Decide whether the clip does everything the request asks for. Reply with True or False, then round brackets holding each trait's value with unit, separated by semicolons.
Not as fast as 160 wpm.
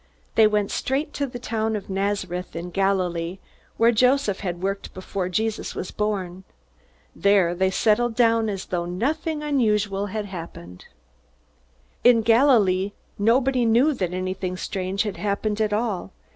True (145 wpm)